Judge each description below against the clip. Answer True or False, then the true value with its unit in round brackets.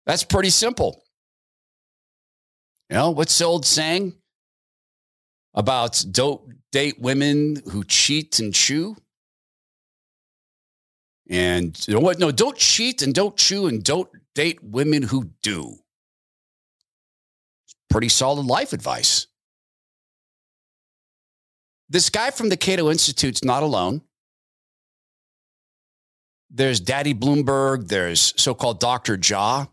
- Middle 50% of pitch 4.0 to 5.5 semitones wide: True (5.2 semitones)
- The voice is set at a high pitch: False (140 Hz)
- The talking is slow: True (110 wpm)